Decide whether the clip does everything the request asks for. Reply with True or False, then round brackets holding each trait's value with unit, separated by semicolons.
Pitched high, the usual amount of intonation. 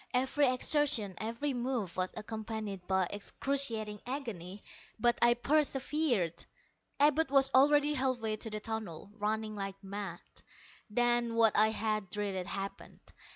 True (225 Hz; 4.4 semitones)